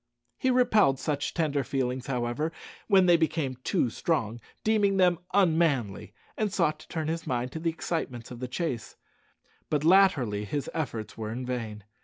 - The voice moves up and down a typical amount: No, wide, 5.7 semitones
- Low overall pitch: No, medium, 145 Hz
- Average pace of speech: Yes, average, 165 wpm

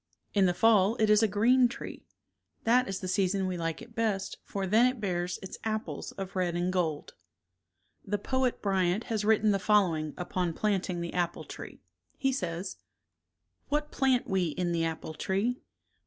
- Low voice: No, high, 195 Hz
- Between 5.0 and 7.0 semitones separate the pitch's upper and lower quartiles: No, average, 3.7 semitones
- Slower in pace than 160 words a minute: No, average, 175 wpm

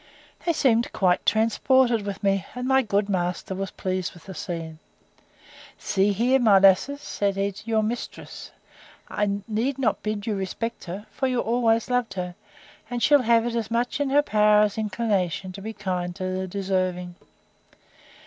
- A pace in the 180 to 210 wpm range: No, average, 170 wpm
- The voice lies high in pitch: Yes, high, 210 Hz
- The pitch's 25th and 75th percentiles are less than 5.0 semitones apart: Yes, average, 3.7 semitones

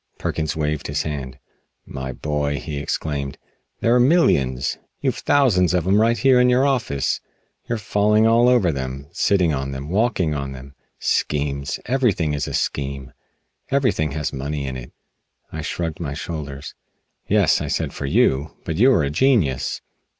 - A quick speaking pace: No, average, 160 wpm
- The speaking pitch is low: Yes, very low, 75 Hz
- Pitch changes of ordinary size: No, wide, 7.8 semitones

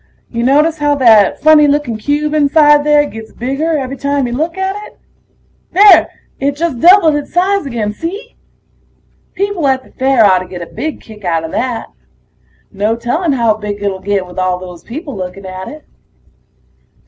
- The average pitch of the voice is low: No, very high, 270 Hz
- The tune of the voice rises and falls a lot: Yes, wide, 6.5 semitones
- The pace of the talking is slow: No, average, 170 wpm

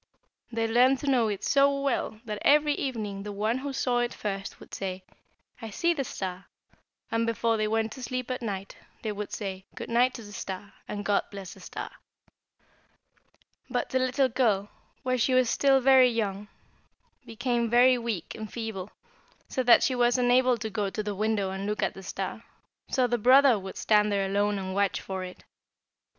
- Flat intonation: No, average, 3.9 semitones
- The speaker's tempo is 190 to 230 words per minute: Yes, average, 195 wpm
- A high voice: Yes, high, 225 Hz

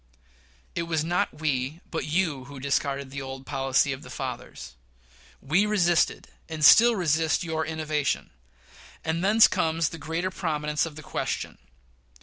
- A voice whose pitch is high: No, medium, 155 Hz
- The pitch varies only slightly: No, average, 3.3 semitones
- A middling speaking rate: Yes, average, 145 wpm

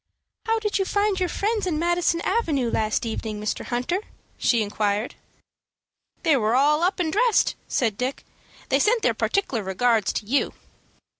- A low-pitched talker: No, very high, 295 Hz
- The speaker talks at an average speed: Yes, average, 160 wpm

